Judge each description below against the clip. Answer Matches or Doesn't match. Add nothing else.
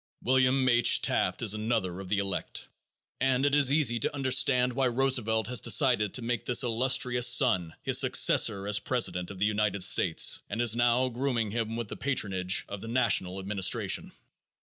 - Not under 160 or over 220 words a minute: Matches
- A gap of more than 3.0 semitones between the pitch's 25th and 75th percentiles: Matches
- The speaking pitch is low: Matches